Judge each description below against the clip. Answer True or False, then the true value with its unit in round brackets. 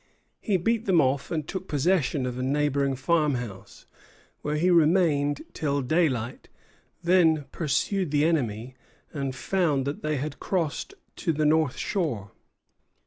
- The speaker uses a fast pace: False (140 wpm)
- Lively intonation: False (3.9 semitones)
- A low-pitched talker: False (150 Hz)